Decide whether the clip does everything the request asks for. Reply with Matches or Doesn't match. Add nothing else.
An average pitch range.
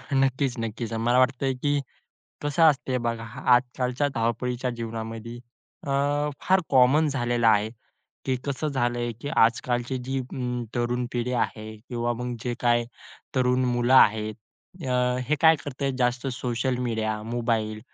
Doesn't match